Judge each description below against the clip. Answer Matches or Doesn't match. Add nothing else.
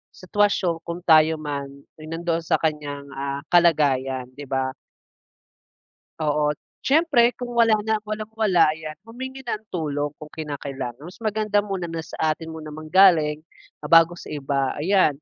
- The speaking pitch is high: Doesn't match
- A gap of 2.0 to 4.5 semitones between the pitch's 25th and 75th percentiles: Doesn't match